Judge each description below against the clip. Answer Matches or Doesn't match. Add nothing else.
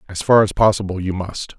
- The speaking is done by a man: Matches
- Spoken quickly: Matches